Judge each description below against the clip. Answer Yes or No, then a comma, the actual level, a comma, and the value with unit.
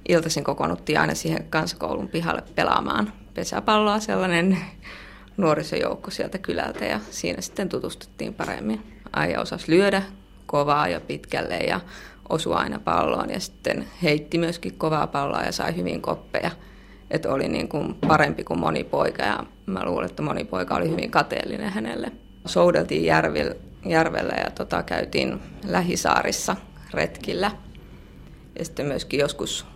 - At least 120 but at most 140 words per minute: Yes, average, 135 wpm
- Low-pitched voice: No, medium, 165 Hz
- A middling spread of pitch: Yes, average, 4.3 semitones